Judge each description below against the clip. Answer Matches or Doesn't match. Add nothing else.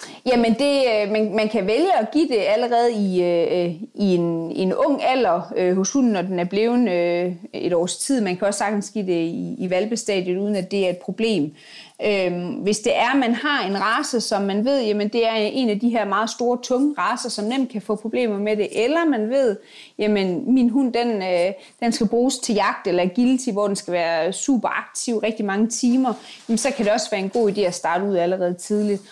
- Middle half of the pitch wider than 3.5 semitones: Matches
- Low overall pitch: Doesn't match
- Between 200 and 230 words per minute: Matches